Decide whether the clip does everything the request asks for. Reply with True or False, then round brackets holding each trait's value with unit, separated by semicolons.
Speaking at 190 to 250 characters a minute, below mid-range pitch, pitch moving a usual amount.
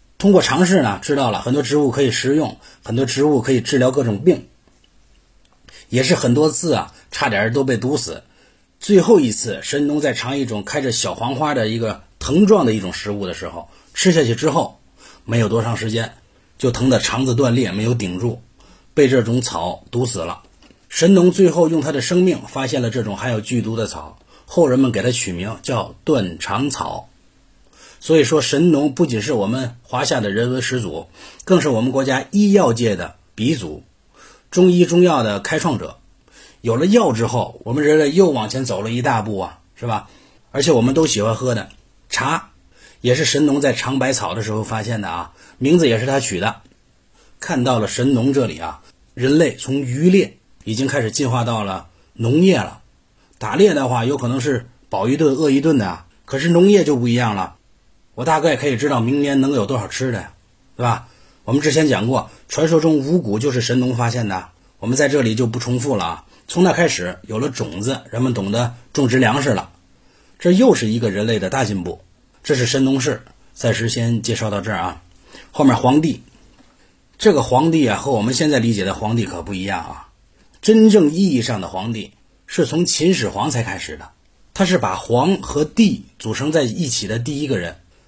False (280 characters per minute; 125 Hz; 4.9 semitones)